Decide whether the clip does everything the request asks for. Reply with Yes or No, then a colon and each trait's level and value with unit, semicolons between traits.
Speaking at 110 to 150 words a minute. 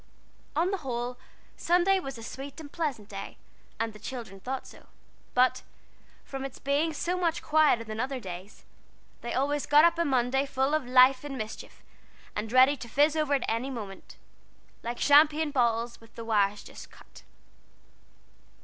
No: average, 165 wpm